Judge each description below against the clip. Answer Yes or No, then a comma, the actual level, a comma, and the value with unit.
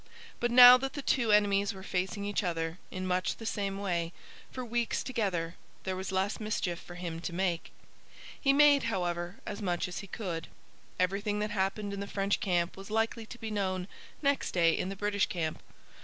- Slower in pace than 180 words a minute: No, average, 195 wpm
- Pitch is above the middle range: Yes, high, 195 Hz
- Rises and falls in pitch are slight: No, average, 3.0 semitones